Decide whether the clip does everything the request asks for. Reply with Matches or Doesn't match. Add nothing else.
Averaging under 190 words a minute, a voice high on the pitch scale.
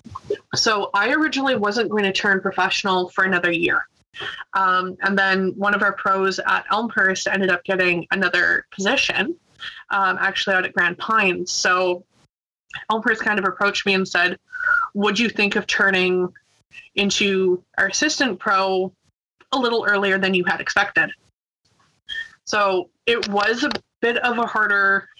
Matches